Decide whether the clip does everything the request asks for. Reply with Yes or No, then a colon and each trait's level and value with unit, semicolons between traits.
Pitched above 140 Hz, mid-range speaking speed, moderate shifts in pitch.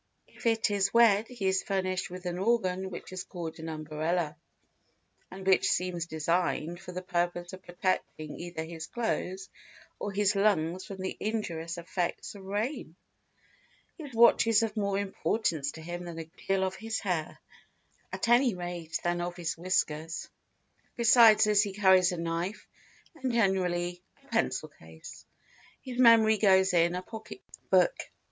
Yes: medium, 185 Hz; average, 160 wpm; average, 3.3 semitones